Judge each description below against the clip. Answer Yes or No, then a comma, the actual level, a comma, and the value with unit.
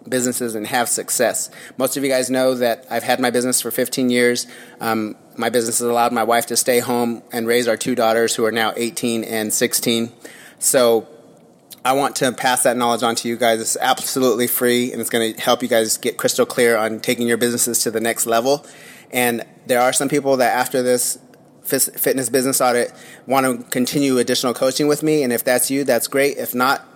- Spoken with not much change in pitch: Yes, narrow, 1.6 semitones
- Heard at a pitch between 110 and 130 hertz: Yes, low, 120 Hz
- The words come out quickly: Yes, fast, 215 wpm